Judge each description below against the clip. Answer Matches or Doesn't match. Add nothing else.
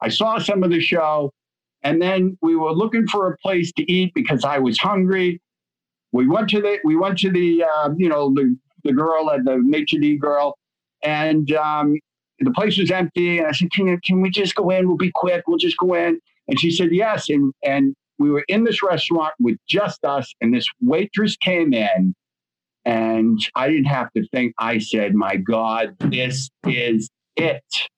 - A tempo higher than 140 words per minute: Matches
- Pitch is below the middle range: Doesn't match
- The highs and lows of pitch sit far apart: Matches